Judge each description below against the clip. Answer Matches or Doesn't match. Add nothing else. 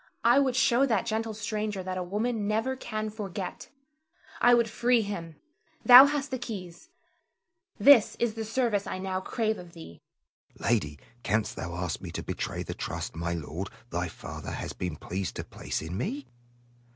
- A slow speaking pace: Doesn't match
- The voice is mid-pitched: Doesn't match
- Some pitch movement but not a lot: Doesn't match